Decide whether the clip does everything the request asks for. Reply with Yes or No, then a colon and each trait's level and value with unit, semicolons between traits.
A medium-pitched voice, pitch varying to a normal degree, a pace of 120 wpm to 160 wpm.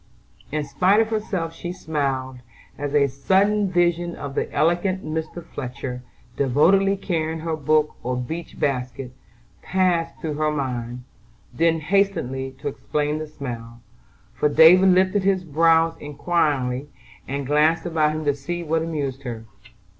Yes: medium, 155 Hz; average, 3.9 semitones; average, 140 wpm